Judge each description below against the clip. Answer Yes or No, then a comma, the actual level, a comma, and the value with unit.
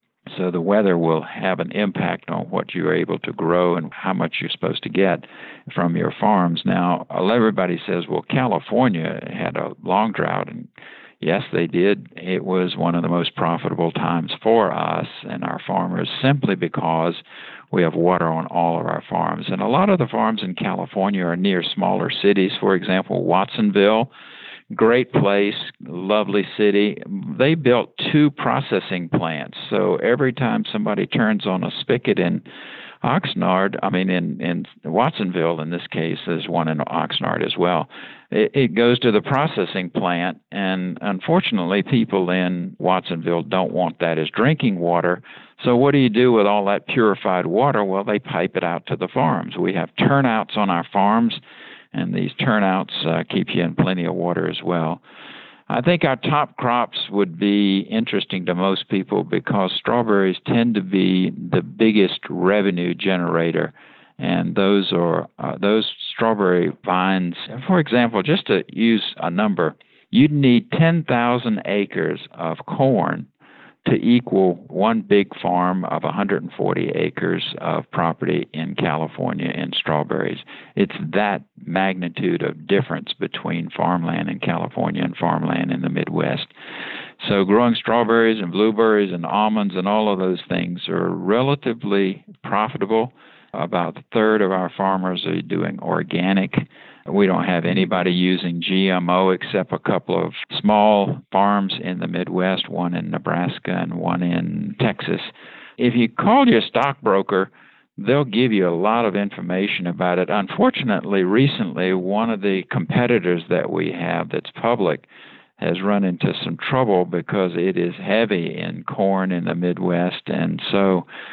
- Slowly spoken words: No, average, 155 wpm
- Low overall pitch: Yes, low, 100 Hz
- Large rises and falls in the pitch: No, average, 3.9 semitones